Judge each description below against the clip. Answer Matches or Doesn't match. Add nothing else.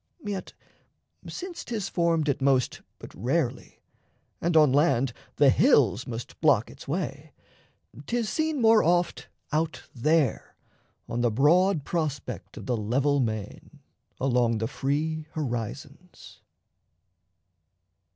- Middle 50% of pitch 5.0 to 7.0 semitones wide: Matches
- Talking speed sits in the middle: Doesn't match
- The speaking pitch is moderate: Matches